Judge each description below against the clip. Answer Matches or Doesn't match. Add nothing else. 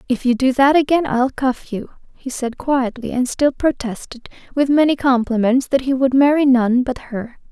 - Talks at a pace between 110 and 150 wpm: Doesn't match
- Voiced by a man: Doesn't match